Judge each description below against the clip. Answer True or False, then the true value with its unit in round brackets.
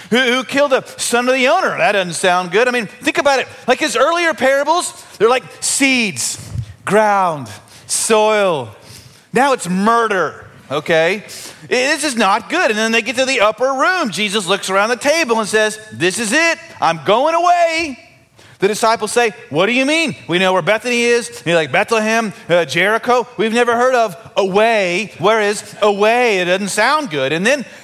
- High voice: True (220 Hz)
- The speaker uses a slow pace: False (185 wpm)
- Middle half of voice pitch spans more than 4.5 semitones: True (5.6 semitones)